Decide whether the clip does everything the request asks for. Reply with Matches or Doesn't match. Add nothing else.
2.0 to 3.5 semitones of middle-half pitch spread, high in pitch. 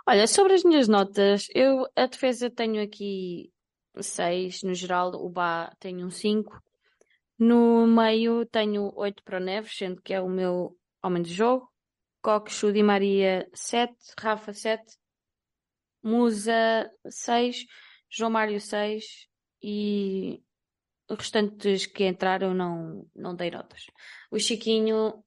Matches